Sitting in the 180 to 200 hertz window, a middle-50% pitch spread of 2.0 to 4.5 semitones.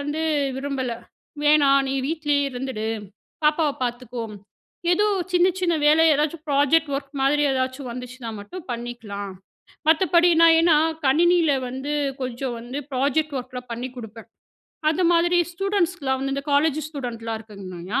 No: very high, 275 Hz; average, 4.2 semitones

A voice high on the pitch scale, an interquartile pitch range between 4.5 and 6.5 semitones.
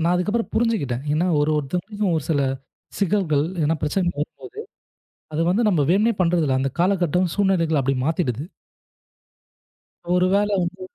No: medium, 175 Hz; average, 5.0 semitones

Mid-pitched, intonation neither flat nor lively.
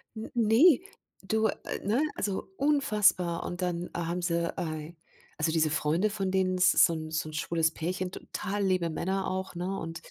Yes: medium, 180 Hz; average, 3.2 semitones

